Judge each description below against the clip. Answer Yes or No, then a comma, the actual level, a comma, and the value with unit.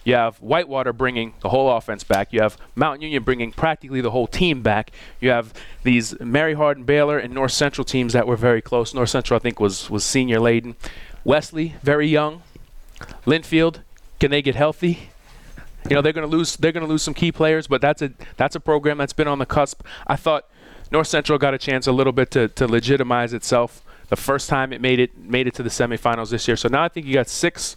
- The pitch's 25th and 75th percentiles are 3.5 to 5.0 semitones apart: Yes, average, 3.9 semitones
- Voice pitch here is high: No, low, 135 Hz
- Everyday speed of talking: No, fast, 220 wpm